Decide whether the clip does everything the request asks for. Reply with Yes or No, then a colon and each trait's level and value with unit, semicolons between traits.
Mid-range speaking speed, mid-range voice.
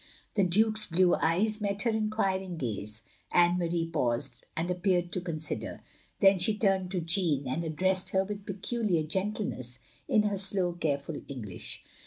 Yes: average, 155 wpm; medium, 180 Hz